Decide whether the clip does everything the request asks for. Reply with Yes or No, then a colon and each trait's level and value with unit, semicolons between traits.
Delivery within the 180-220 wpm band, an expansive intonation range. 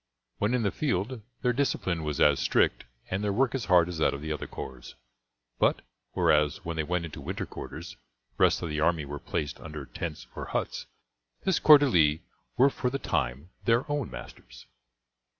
Yes: average, 190 wpm; wide, 8.1 semitones